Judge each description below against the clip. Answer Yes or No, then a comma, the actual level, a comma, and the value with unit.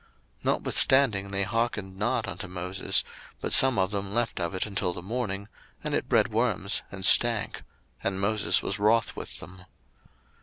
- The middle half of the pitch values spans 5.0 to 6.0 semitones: No, average, 3.1 semitones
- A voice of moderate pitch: No, low, 100 Hz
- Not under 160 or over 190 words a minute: Yes, average, 165 wpm